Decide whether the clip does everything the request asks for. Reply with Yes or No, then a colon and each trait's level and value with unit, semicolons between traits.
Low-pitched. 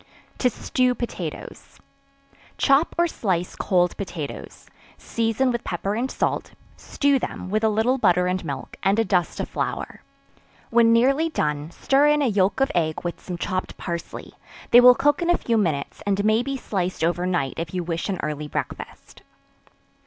No: high, 200 Hz